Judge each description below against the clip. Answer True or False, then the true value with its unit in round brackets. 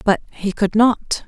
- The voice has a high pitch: True (210 Hz)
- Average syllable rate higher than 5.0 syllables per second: False (3.7 syllables/s)